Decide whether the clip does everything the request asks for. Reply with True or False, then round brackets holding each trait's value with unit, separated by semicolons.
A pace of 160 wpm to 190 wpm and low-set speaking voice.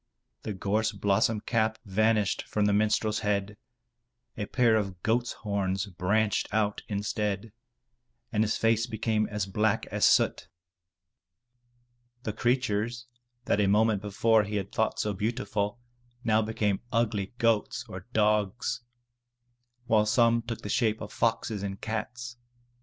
False (135 wpm; 105 Hz)